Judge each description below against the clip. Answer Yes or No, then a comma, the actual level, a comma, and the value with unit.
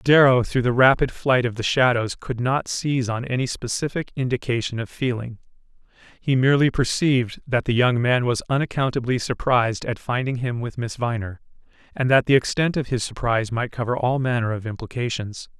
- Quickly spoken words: No, average, 175 wpm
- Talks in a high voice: No, low, 125 Hz